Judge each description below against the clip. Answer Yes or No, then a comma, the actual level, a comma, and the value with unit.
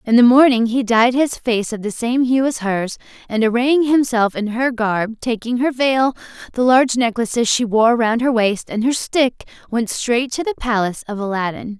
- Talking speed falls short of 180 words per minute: No, fast, 205 wpm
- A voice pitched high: Yes, high, 235 Hz